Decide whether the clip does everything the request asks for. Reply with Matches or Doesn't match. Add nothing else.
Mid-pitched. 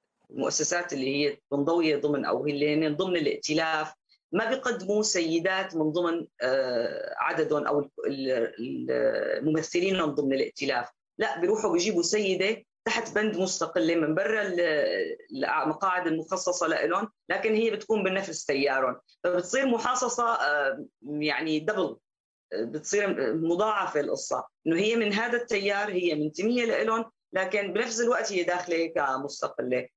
Matches